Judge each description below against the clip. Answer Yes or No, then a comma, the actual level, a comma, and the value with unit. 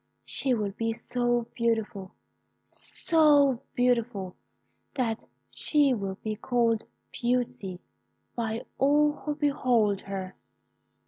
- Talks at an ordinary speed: No, slow, 95 wpm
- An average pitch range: Yes, average, 3.6 semitones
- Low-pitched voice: No, high, 235 Hz